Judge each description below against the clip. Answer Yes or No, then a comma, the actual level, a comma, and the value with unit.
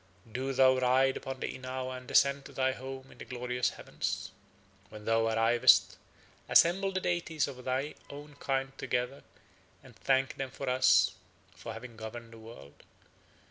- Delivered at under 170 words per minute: Yes, average, 160 wpm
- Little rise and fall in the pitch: Yes, narrow, 1.8 semitones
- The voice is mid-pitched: No, low, 130 Hz